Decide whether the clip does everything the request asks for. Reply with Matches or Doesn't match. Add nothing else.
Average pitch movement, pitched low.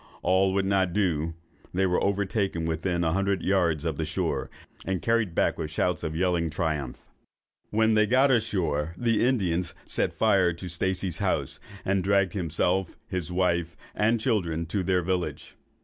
Matches